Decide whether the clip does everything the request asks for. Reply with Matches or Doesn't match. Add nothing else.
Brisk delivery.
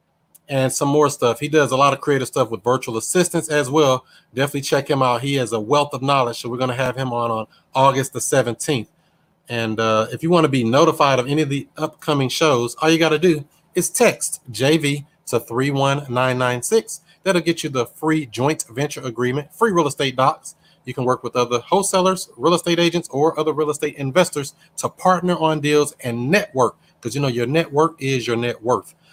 Matches